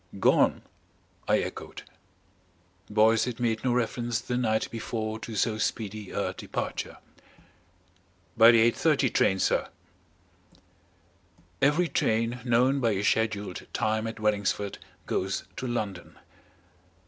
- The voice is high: No, low, 110 Hz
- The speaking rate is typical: No, slow, 115 wpm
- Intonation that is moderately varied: No, narrow, 1.9 semitones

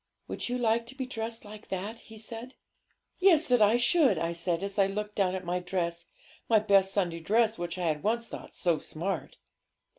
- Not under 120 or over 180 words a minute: No, fast, 205 wpm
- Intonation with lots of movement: No, average, 4.3 semitones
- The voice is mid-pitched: No, high, 205 Hz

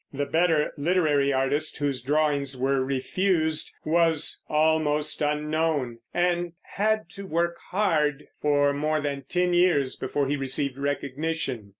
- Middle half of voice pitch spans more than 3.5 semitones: No, average, 2.7 semitones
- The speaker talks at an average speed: No, slow, 125 wpm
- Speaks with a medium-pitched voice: Yes, medium, 150 Hz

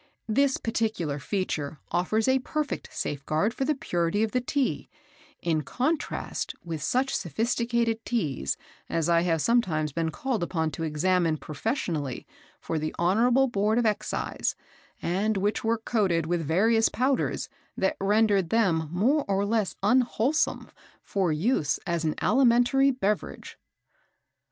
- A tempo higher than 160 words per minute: No, slow, 135 wpm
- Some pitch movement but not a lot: No, wide, 6.2 semitones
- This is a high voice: Yes, high, 205 Hz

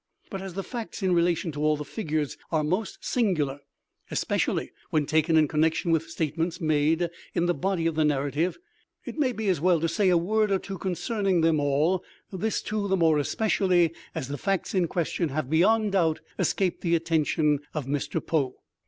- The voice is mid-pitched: Yes, medium, 170 Hz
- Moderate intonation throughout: Yes, average, 3.8 semitones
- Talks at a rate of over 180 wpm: Yes, average, 190 wpm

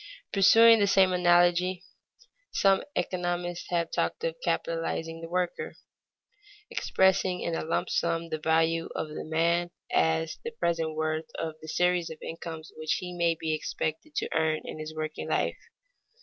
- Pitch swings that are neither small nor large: No, narrow, 2.0 semitones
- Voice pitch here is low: No, medium, 170 Hz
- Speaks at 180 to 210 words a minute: No, average, 155 wpm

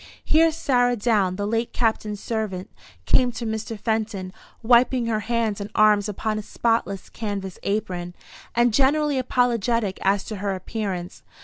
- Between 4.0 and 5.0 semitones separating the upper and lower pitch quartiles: No, average, 3.0 semitones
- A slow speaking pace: No, average, 145 wpm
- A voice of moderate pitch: No, high, 220 Hz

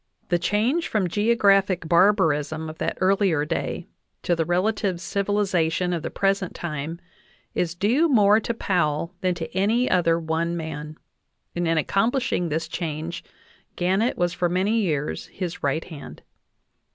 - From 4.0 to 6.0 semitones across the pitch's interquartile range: No, average, 3.6 semitones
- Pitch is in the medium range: Yes, medium, 175 Hz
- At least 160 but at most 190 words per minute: No, average, 150 wpm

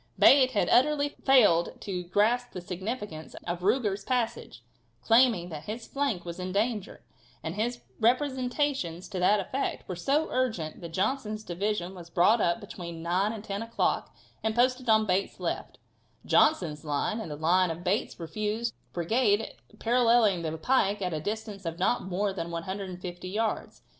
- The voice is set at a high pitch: Yes, high, 205 Hz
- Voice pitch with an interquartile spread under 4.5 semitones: No, average, 4.9 semitones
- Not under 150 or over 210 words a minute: Yes, average, 160 wpm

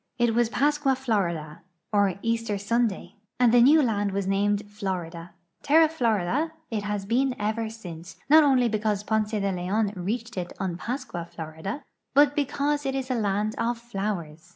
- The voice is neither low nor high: No, high, 215 Hz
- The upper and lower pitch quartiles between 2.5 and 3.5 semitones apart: No, average, 4.1 semitones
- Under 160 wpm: No, average, 170 wpm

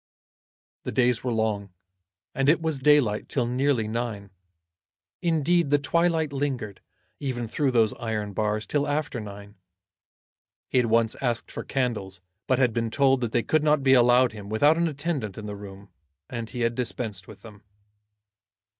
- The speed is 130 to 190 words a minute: Yes, average, 165 wpm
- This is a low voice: Yes, low, 120 Hz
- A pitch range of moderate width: Yes, average, 4.7 semitones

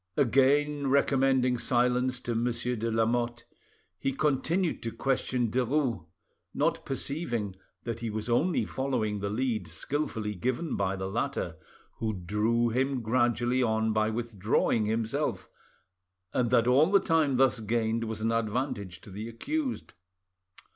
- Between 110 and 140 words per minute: Yes, slow, 135 wpm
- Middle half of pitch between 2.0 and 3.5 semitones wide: Yes, average, 3.2 semitones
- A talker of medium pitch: No, low, 120 Hz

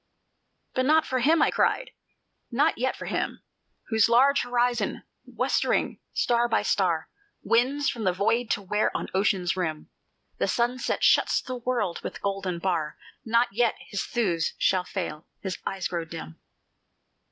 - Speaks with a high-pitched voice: Yes, high, 220 Hz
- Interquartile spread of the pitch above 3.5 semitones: Yes, average, 5.0 semitones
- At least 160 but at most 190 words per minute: No, average, 150 wpm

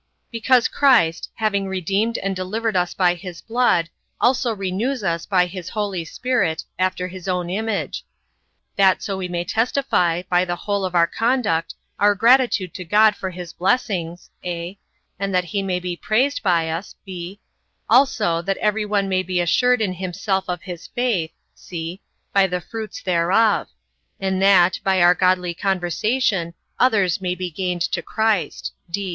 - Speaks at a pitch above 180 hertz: Yes, high, 190 Hz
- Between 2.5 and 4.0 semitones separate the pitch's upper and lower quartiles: Yes, average, 3.3 semitones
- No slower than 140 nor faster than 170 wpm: Yes, average, 160 wpm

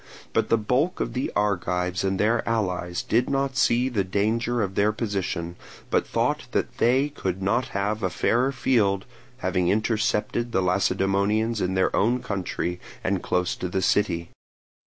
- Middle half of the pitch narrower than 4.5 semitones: Yes, average, 3.9 semitones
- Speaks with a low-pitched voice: Yes, low, 105 Hz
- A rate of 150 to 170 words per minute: Yes, average, 160 wpm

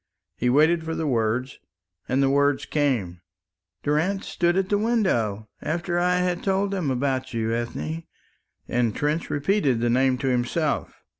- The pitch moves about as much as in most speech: No, wide, 6.0 semitones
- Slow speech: No, average, 155 wpm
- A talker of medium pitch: Yes, medium, 145 Hz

